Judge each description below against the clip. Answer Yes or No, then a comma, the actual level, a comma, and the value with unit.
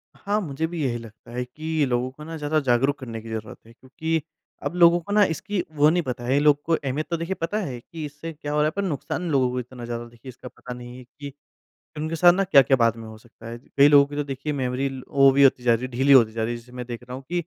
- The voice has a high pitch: No, low, 135 Hz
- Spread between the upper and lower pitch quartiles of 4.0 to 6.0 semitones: Yes, average, 4.3 semitones